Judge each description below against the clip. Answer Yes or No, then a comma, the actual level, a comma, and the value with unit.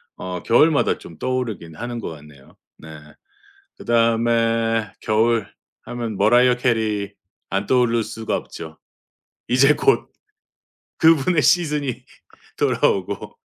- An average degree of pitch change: Yes, average, 3.7 semitones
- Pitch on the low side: Yes, low, 115 Hz